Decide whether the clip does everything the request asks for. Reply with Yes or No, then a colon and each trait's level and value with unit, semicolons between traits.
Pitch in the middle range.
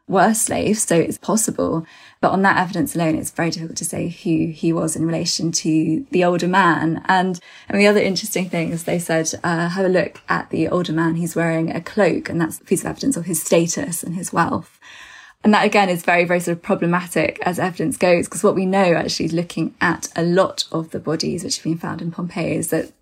Yes: medium, 175 Hz